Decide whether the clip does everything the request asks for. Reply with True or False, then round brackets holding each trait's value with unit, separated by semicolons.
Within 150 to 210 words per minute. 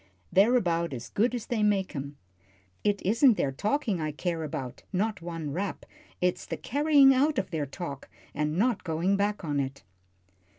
True (175 wpm)